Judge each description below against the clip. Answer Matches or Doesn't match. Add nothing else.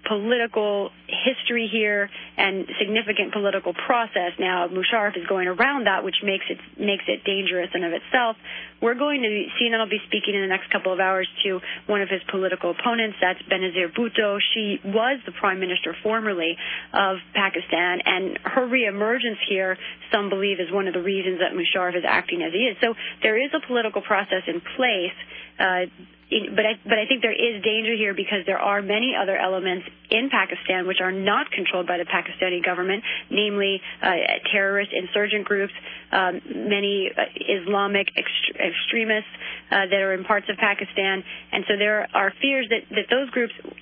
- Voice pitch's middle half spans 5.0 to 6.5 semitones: Doesn't match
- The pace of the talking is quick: Doesn't match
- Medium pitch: Doesn't match